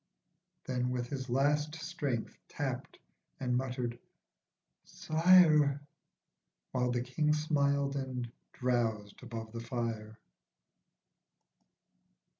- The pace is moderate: No, slow, 85 wpm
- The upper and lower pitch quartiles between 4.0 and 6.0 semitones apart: No, average, 3.4 semitones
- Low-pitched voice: Yes, low, 130 Hz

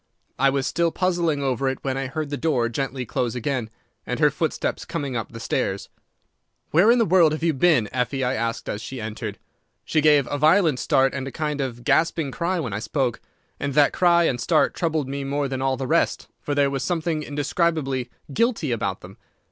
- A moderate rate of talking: No, fast, 210 wpm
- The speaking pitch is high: No, medium, 140 Hz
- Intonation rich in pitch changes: No, average, 3.9 semitones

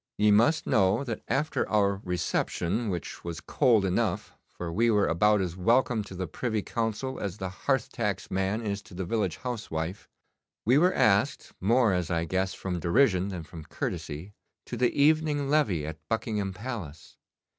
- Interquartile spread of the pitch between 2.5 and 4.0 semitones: No, average, 4.7 semitones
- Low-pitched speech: Yes, low, 100 Hz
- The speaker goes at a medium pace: Yes, average, 170 wpm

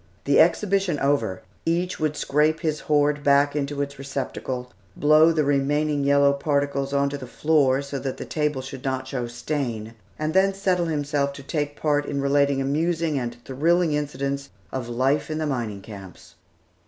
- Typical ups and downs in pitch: No, narrow, 2.0 semitones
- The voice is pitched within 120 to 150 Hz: Yes, medium, 140 Hz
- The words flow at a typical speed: Yes, average, 175 wpm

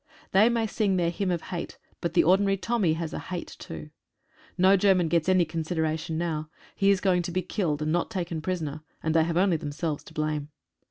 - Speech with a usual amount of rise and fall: Yes, average, 3.0 semitones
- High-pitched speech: No, medium, 170 Hz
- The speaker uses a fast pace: Yes, fast, 210 wpm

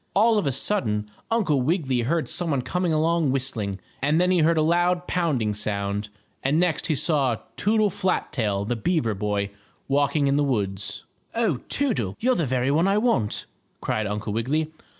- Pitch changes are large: Yes, wide, 7.8 semitones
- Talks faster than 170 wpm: Yes, average, 180 wpm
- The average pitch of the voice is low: No, medium, 145 Hz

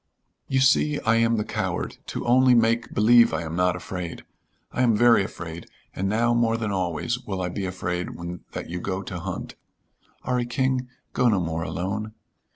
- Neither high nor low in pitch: No, low, 105 Hz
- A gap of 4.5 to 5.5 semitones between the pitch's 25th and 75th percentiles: Yes, average, 4.9 semitones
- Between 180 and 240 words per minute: Yes, average, 185 wpm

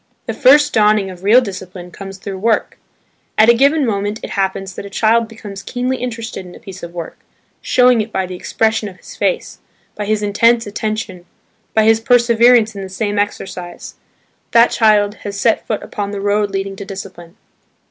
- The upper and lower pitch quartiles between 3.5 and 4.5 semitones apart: No, average, 2.8 semitones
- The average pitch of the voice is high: Yes, high, 210 Hz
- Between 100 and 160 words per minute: No, average, 190 wpm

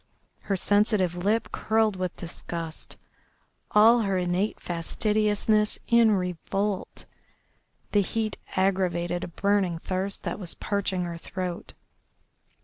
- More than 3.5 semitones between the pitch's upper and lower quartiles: No, average, 3.0 semitones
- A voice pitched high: Yes, high, 195 Hz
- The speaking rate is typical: No, slow, 110 wpm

